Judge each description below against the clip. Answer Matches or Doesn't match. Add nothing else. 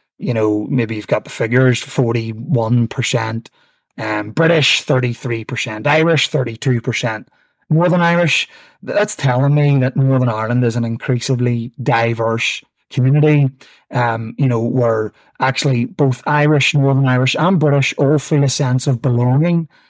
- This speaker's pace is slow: Matches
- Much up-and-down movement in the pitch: Doesn't match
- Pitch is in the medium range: Doesn't match